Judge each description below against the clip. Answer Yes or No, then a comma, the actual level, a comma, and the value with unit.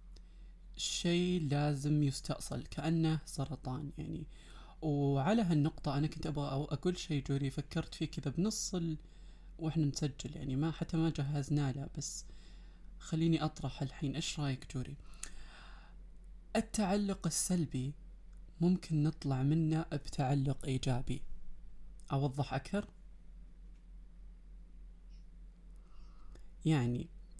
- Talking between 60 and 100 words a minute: Yes, average, 90 wpm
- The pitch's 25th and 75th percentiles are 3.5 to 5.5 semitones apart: No, average, 3.1 semitones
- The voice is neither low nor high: Yes, medium, 155 Hz